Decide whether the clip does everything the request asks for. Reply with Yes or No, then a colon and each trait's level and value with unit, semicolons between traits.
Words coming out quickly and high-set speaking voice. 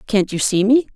Yes: fast, 250 wpm; high, 215 Hz